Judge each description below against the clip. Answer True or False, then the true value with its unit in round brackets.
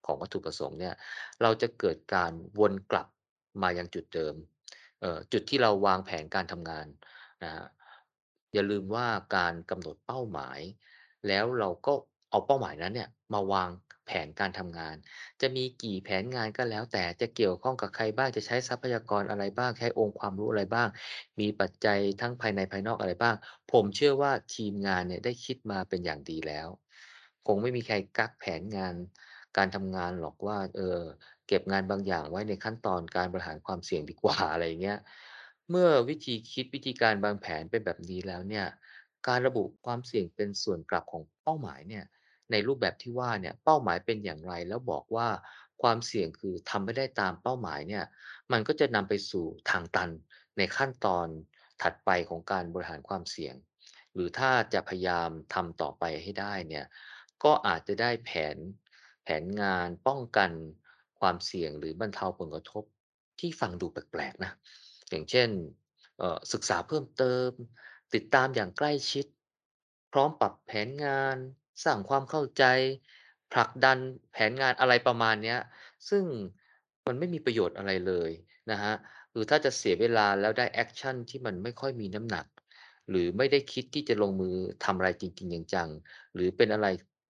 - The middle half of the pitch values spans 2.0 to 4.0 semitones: False (5.2 semitones)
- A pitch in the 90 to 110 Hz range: True (105 Hz)